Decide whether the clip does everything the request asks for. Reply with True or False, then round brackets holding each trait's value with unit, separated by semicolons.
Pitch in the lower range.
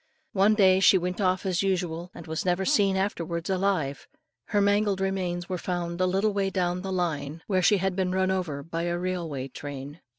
False (185 Hz)